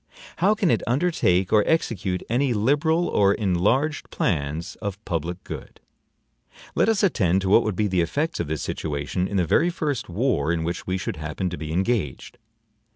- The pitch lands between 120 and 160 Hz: No, low, 100 Hz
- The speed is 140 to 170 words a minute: No, average, 180 wpm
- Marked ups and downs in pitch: Yes, wide, 8.0 semitones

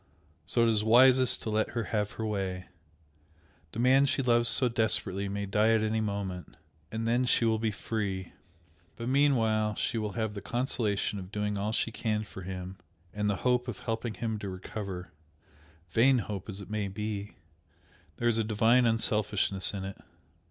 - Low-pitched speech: Yes, low, 110 Hz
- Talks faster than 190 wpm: No, average, 180 wpm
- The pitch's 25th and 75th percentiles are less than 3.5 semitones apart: Yes, narrow, 2.5 semitones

